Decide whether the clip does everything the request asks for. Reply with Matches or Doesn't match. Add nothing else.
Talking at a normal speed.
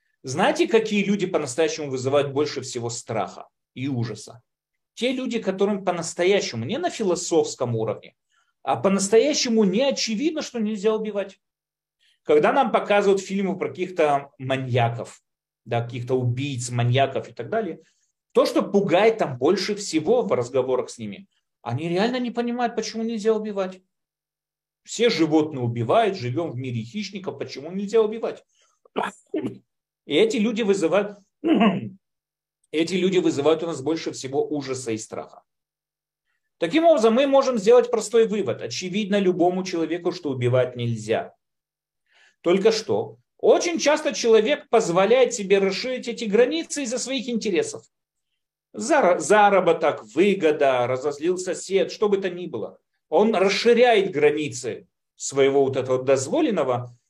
Matches